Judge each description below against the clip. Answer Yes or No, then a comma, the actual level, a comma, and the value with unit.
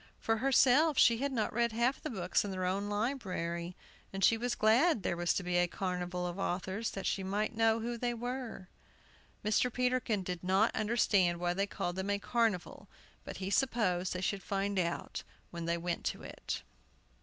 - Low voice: No, high, 200 Hz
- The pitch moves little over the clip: No, average, 4.5 semitones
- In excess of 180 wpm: Yes, average, 190 wpm